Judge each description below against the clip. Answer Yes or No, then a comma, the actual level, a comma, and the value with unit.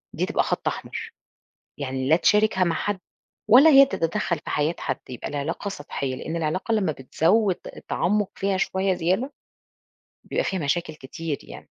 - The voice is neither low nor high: Yes, medium, 175 Hz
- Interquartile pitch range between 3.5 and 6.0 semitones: Yes, wide, 5.4 semitones